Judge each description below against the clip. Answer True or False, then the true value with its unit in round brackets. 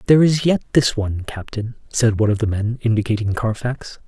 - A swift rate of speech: False (190 wpm)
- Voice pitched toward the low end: True (115 Hz)